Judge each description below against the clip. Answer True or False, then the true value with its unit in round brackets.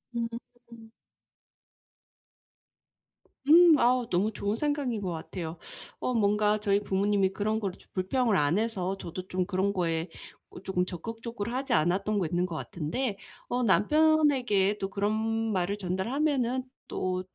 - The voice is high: True (205 Hz)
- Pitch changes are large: False (4.5 semitones)